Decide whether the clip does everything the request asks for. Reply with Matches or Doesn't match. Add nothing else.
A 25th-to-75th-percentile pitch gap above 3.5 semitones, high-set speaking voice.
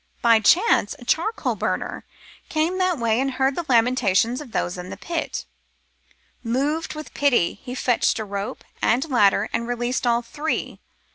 Matches